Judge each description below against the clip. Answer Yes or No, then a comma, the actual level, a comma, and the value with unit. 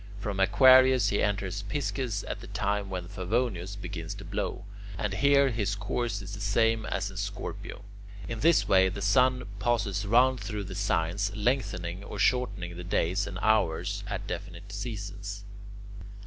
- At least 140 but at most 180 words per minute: Yes, average, 160 wpm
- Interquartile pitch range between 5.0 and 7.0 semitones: No, average, 3.3 semitones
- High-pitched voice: No, low, 100 Hz